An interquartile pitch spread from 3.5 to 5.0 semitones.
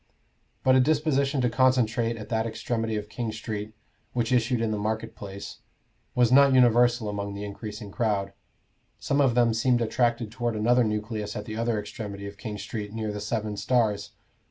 No: narrow, 2.6 semitones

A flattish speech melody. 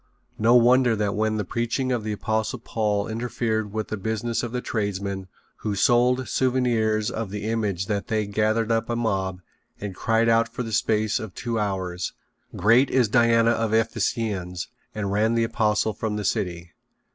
Yes: narrow, 2.1 semitones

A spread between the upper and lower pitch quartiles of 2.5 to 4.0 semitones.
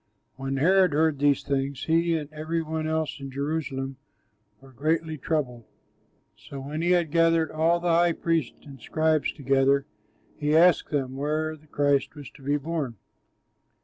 Yes: average, 2.8 semitones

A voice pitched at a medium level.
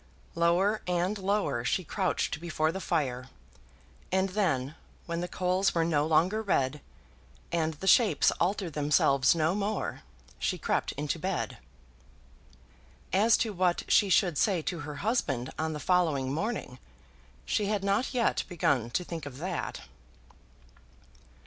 Yes: medium, 175 Hz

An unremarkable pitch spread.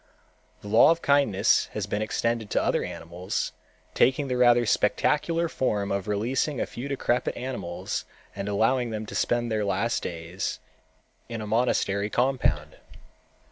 Yes: average, 3.9 semitones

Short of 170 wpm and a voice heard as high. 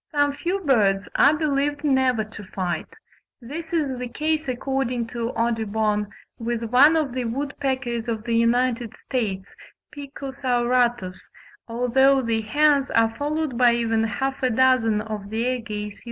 Yes: average, 150 wpm; high, 245 Hz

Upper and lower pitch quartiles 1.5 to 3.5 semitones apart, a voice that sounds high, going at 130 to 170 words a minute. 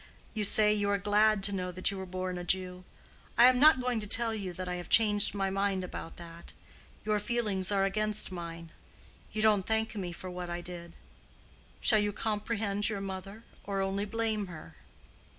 No: average, 2.7 semitones; high, 200 Hz; average, 195 wpm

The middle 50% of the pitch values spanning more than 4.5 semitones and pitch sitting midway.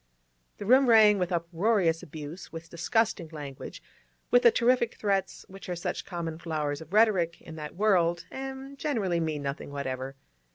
Yes: average, 5.2 semitones; medium, 175 Hz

